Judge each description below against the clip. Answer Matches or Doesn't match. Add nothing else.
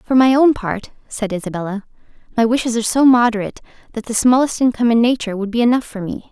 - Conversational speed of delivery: Doesn't match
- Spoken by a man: Doesn't match